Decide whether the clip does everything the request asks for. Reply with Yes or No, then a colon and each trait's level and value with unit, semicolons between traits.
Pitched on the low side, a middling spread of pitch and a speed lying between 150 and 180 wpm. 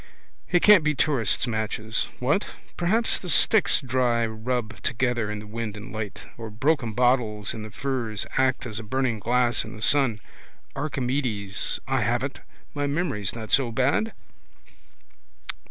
Yes: low, 120 Hz; average, 3.9 semitones; average, 155 wpm